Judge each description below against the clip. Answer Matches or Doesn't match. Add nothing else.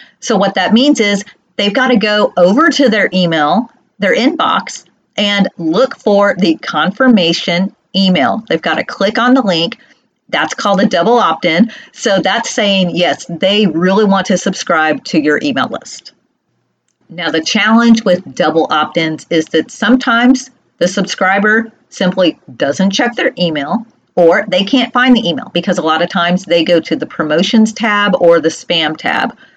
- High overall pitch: Matches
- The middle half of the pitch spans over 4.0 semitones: Matches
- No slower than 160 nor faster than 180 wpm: Matches